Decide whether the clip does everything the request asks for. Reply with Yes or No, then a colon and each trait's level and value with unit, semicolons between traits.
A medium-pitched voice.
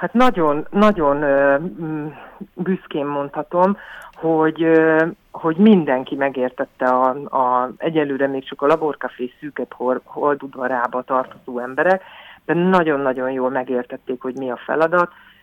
Yes: medium, 145 Hz